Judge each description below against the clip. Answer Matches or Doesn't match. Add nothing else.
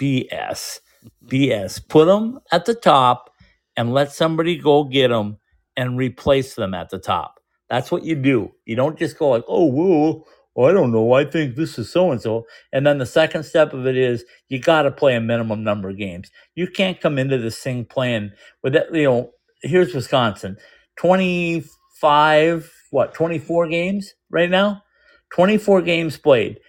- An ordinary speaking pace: Matches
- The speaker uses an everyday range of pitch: Doesn't match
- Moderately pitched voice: Matches